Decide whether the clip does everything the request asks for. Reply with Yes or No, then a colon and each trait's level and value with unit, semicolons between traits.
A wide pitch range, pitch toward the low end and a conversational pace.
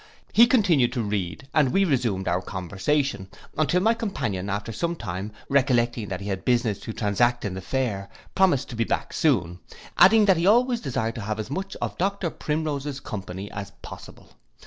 Yes: wide, 8.1 semitones; low, 120 Hz; average, 185 wpm